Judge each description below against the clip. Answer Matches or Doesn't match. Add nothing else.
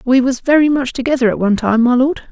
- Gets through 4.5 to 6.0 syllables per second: Doesn't match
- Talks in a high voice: Matches